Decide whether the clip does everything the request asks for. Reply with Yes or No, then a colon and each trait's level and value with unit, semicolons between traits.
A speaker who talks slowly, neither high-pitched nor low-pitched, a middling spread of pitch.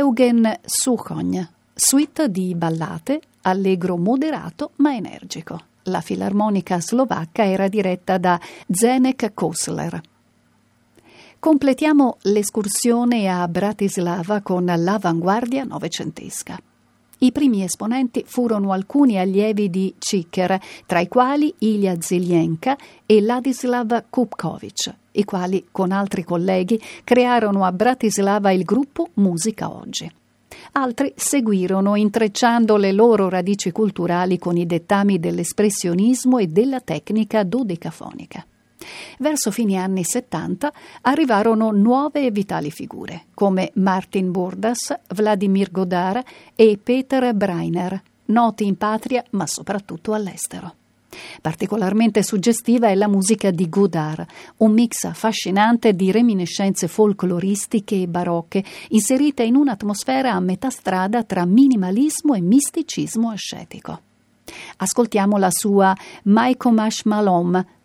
No: slow, 105 wpm; high, 210 Hz; average, 4.5 semitones